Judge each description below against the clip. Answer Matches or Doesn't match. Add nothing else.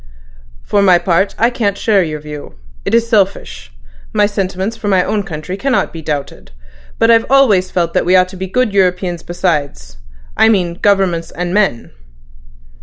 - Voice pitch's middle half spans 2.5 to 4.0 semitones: Matches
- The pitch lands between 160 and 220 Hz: Matches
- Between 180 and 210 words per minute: Doesn't match